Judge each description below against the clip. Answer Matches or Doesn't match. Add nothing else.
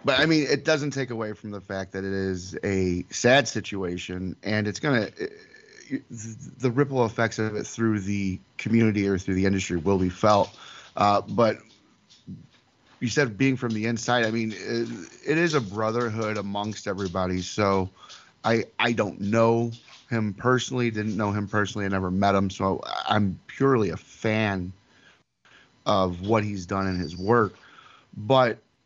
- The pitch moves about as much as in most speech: Matches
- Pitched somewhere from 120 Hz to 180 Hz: Doesn't match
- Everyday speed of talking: Matches